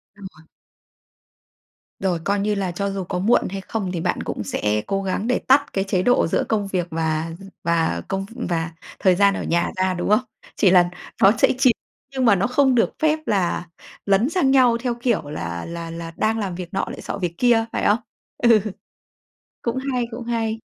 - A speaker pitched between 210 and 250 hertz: No, high, 195 Hz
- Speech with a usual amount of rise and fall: Yes, average, 4.7 semitones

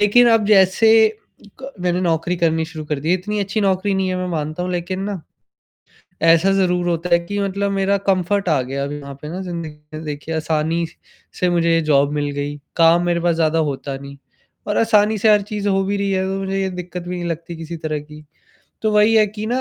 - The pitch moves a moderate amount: Yes, average, 3.6 semitones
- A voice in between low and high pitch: Yes, medium, 180 Hz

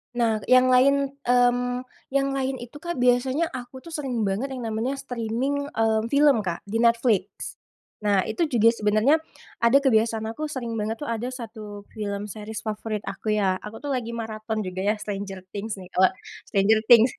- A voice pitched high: Yes, high, 230 Hz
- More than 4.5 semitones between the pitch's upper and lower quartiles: No, average, 3.3 semitones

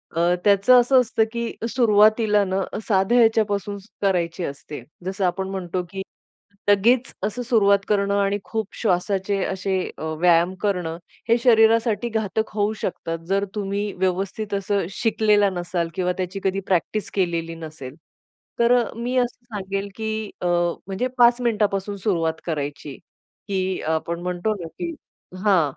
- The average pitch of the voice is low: No, high, 200 Hz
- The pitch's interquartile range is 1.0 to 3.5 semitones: Yes, average, 3.2 semitones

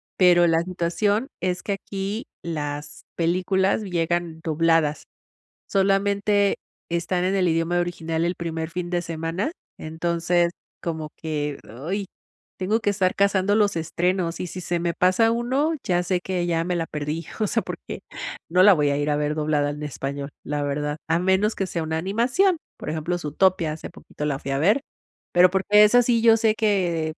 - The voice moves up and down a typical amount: Yes, average, 3.4 semitones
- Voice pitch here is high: No, medium, 175 Hz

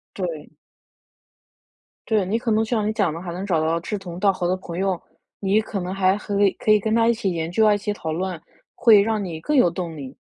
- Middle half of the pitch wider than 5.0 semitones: No, average, 3.6 semitones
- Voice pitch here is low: No, high, 195 Hz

